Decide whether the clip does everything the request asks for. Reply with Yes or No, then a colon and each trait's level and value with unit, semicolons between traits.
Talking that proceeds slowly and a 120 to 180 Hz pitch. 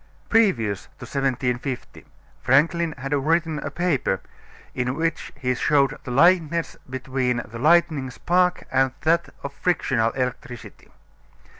Yes: slow, 120 wpm; medium, 140 Hz